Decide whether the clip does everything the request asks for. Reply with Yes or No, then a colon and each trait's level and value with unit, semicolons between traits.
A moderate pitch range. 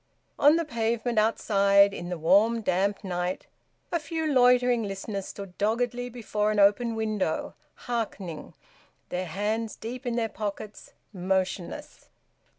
Yes: average, 3.3 semitones